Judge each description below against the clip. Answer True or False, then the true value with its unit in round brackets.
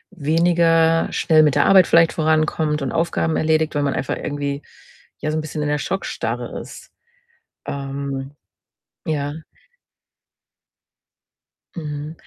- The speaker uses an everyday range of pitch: False (2.1 semitones)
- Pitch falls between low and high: True (155 Hz)